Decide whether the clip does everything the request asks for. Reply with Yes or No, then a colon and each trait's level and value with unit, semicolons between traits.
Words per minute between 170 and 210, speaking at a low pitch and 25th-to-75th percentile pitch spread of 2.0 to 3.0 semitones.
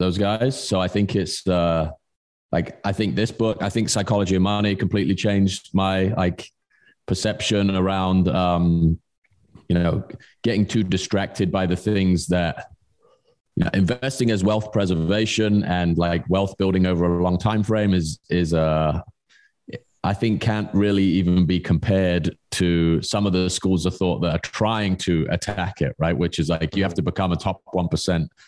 Yes: average, 175 wpm; very low, 95 Hz; average, 2.7 semitones